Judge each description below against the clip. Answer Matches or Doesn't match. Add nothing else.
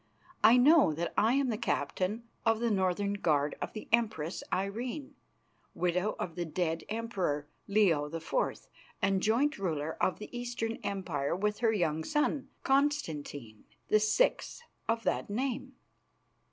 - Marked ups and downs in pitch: Matches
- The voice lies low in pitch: Doesn't match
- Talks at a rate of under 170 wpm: Matches